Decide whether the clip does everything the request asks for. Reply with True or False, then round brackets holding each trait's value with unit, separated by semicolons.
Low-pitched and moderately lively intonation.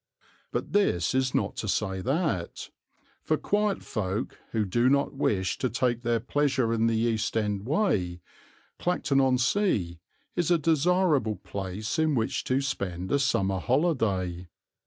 False (120 Hz; 6.8 semitones)